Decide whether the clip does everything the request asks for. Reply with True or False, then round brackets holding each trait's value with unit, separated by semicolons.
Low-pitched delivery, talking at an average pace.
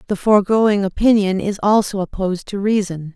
False (200 Hz; 150 wpm)